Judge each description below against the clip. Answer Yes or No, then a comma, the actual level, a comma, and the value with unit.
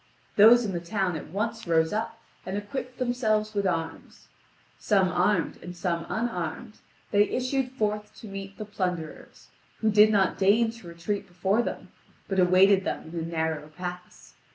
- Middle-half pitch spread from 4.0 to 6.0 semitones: No, average, 3.5 semitones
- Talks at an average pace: Yes, average, 165 wpm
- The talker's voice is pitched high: Yes, high, 195 Hz